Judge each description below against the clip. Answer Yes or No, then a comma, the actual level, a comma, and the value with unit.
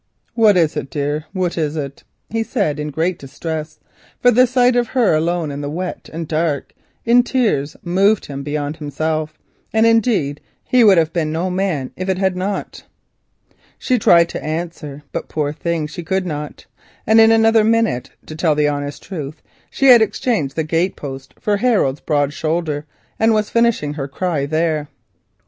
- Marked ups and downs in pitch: Yes, wide, 6.1 semitones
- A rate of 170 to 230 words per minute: Yes, average, 175 wpm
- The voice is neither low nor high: Yes, medium, 165 Hz